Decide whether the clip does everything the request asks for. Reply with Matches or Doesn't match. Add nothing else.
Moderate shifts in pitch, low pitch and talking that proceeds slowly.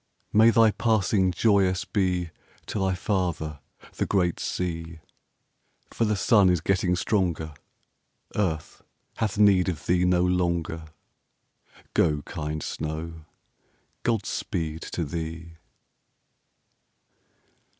Matches